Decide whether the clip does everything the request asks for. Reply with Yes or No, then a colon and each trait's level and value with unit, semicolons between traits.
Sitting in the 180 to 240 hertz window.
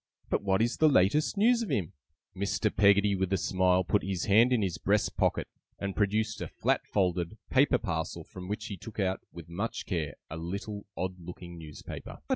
No: very low, 95 Hz